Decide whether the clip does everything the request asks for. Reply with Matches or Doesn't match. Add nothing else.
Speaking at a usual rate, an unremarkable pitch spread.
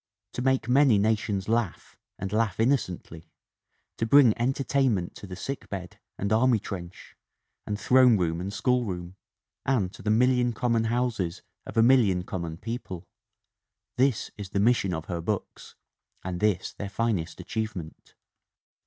Matches